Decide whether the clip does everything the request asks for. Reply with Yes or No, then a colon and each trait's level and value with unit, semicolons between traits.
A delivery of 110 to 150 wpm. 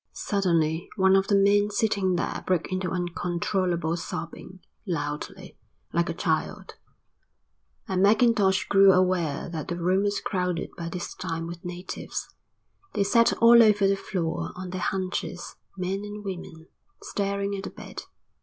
Yes: average, 145 wpm